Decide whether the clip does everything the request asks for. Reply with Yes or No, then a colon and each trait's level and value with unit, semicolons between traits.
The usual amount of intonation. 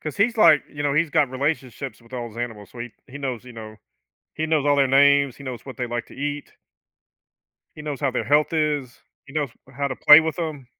Yes: average, 3.1 semitones